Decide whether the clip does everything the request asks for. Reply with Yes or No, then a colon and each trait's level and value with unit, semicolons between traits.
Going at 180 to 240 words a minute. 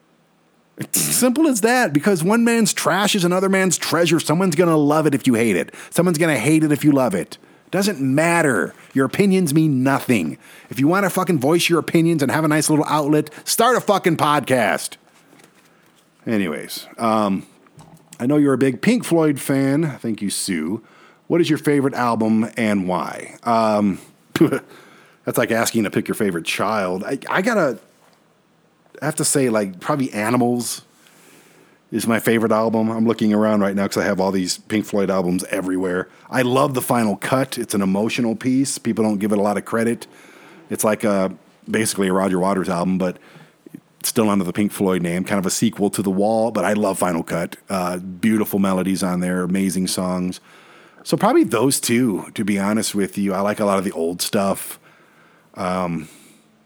Yes: average, 190 wpm